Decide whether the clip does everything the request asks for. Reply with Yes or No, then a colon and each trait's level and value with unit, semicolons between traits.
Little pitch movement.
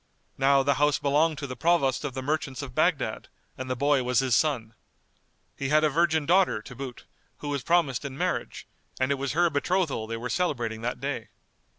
No: average, 3.2 semitones